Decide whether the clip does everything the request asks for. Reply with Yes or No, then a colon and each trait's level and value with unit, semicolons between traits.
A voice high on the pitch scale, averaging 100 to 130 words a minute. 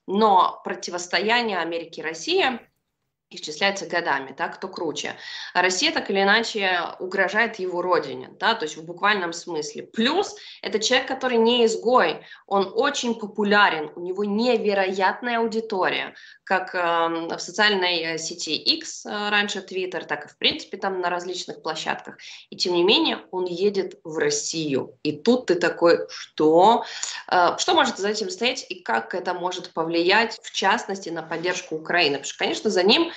No: high, 195 Hz; fast, 160 wpm